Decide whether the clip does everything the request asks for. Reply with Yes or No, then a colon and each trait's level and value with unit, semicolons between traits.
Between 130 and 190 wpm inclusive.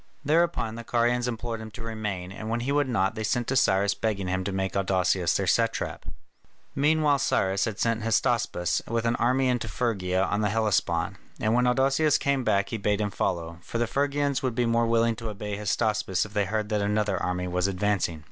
No: fast, 205 wpm